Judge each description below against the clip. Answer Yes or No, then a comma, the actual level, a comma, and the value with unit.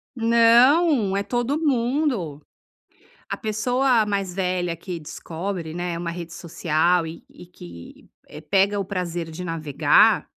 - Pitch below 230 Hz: Yes, medium, 185 Hz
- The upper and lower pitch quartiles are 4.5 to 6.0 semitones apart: Yes, wide, 5.5 semitones